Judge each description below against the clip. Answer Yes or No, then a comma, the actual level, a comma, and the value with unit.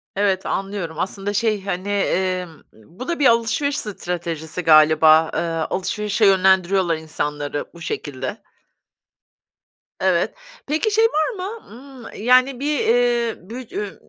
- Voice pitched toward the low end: No, high, 195 Hz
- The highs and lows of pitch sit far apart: Yes, wide, 6.6 semitones